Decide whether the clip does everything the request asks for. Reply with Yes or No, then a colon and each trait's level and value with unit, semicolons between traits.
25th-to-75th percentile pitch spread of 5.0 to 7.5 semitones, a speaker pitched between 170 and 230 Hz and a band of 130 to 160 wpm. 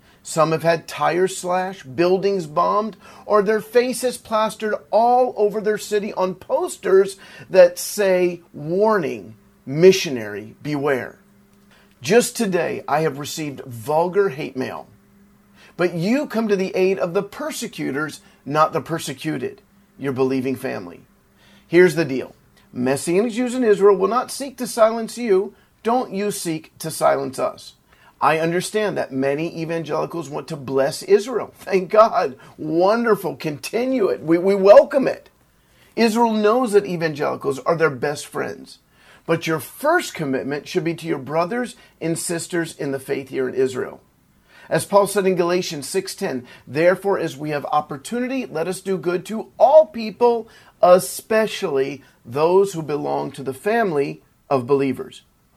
Yes: wide, 5.5 semitones; medium, 185 Hz; average, 145 wpm